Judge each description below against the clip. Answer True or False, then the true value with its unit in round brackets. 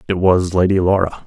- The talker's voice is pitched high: False (95 Hz)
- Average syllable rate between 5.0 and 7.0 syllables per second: True (5.6 syllables/s)